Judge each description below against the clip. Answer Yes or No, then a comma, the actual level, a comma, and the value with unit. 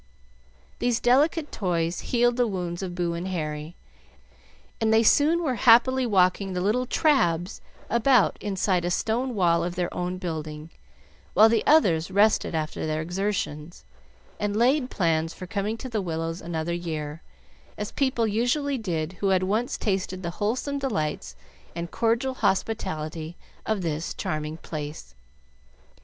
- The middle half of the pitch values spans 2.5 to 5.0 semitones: No, wide, 5.6 semitones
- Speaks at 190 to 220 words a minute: No, average, 145 wpm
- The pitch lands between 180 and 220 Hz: Yes, high, 190 Hz